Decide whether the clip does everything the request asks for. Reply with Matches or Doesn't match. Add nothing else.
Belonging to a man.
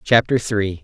Matches